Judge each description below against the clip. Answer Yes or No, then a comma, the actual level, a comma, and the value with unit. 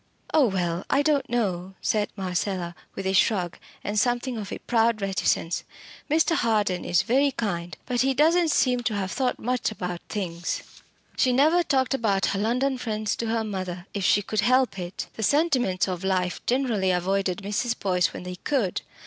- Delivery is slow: No, average, 180 wpm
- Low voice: No, high, 210 Hz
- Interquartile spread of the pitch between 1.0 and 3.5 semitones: No, average, 5.1 semitones